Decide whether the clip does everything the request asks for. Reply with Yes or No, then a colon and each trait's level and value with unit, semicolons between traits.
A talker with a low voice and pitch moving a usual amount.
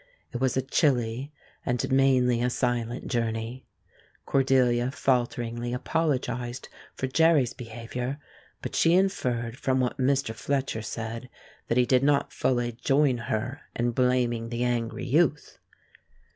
No: low, 125 Hz; narrow, 2.0 semitones